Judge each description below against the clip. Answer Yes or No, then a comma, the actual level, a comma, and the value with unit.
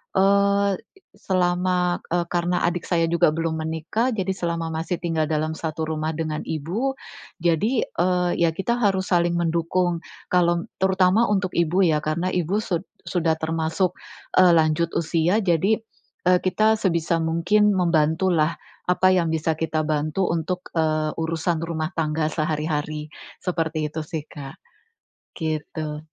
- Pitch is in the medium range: Yes, medium, 170 Hz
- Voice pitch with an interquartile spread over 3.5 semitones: No, narrow, 2.5 semitones